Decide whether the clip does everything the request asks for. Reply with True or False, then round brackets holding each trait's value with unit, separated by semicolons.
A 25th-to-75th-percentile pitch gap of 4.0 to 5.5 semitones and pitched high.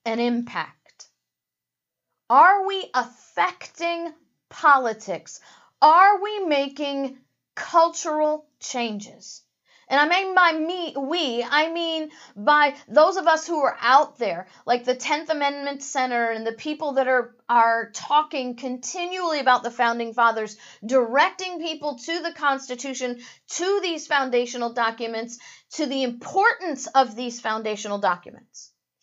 True (4.8 semitones; 275 Hz)